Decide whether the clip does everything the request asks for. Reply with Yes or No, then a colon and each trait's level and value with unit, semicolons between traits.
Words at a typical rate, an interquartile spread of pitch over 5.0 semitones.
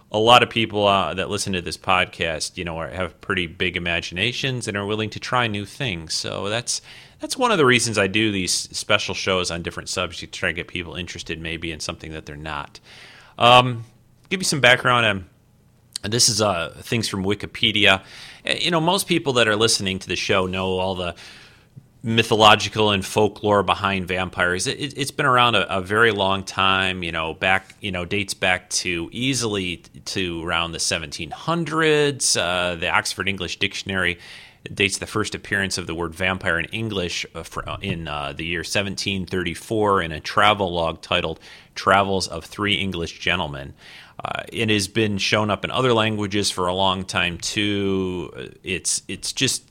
No: average, 185 wpm; average, 4.3 semitones